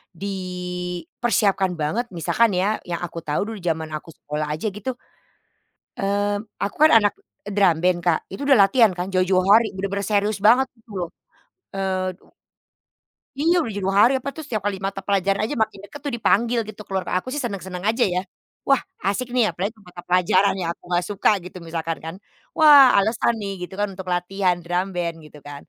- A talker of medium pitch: No, high, 195 Hz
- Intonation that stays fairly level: No, average, 3.4 semitones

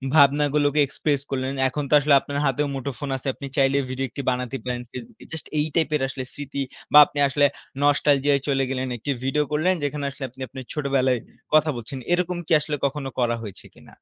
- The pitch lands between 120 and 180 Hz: Yes, medium, 140 Hz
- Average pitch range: No, narrow, 2.0 semitones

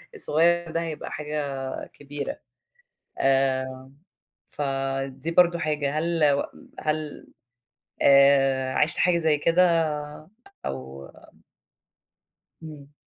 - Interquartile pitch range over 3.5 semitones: No, average, 2.8 semitones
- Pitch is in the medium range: Yes, medium, 145 Hz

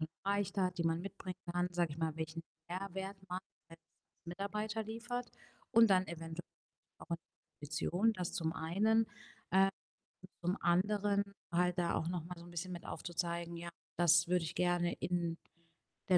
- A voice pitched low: No, medium, 175 Hz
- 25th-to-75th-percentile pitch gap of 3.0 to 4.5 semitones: No, narrow, 2.5 semitones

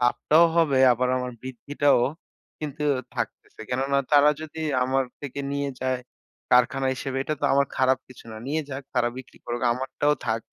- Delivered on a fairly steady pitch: Yes, narrow, 2.2 semitones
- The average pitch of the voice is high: No, low, 135 Hz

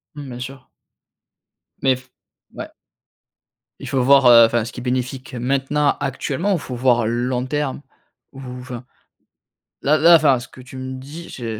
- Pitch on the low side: Yes, low, 130 Hz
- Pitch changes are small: Yes, narrow, 2.0 semitones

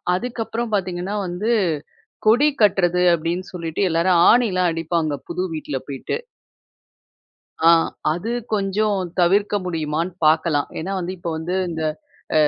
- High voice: No, medium, 180 Hz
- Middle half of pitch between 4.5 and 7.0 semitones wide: No, average, 3.5 semitones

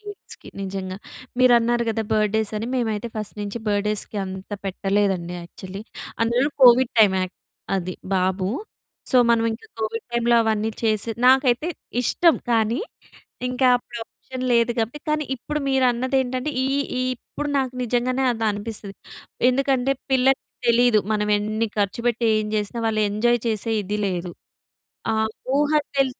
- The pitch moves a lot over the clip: No, average, 3.5 semitones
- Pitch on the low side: No, high, 230 Hz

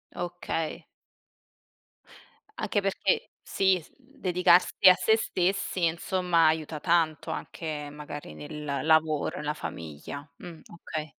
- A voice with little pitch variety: No, average, 3.2 semitones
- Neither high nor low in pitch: Yes, medium, 165 Hz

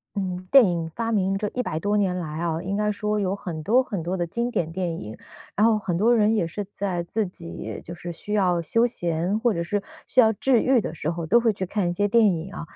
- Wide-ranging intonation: No, average, 3.9 semitones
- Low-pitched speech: No, high, 195 Hz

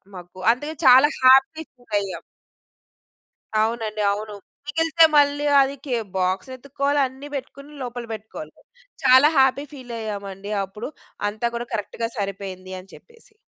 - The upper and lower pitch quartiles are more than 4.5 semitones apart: Yes, average, 5.3 semitones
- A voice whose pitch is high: Yes, high, 245 Hz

